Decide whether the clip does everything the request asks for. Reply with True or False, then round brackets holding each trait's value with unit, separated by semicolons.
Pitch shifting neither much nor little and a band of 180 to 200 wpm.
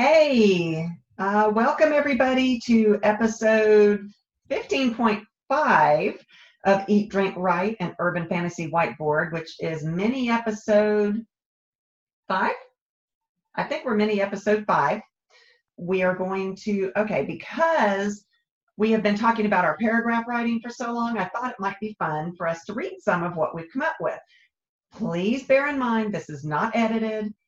False (3.7 semitones; 150 wpm)